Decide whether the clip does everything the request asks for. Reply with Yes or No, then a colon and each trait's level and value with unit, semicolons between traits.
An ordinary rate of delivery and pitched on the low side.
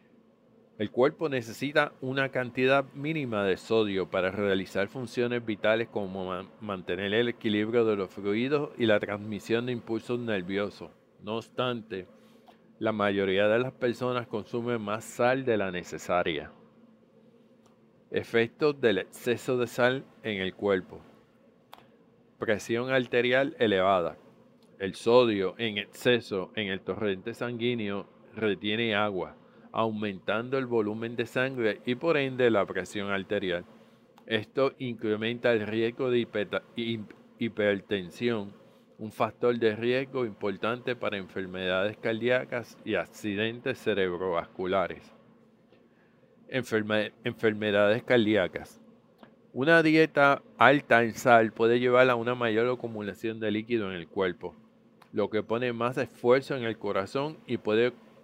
No: slow, 120 wpm; low, 115 Hz